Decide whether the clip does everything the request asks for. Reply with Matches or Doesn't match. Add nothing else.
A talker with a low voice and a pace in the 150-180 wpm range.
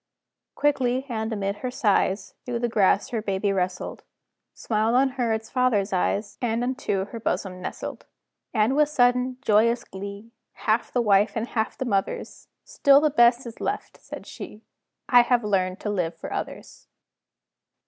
Doesn't match